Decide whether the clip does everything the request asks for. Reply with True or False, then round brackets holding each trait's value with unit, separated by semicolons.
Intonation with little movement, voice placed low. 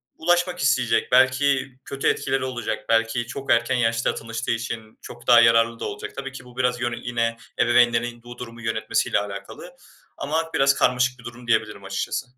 True (2.2 semitones; 120 Hz)